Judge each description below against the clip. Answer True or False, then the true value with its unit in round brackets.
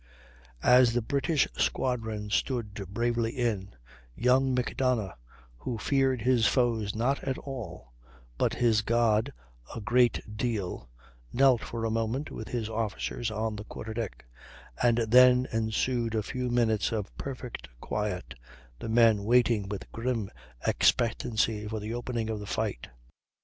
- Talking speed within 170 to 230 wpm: False (140 wpm)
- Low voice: True (115 Hz)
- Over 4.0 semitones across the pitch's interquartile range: False (2.4 semitones)